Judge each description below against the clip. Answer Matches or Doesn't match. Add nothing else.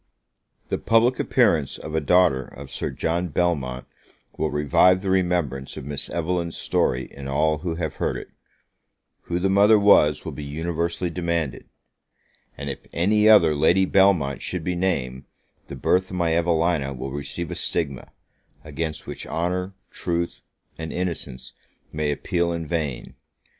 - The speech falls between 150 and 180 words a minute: Matches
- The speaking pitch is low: Matches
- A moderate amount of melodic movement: Matches